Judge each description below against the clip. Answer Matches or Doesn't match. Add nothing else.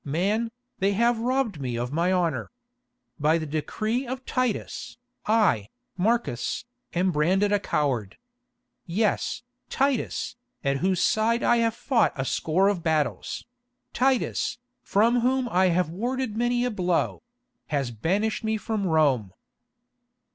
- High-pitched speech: Matches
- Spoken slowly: Matches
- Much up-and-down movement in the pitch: Matches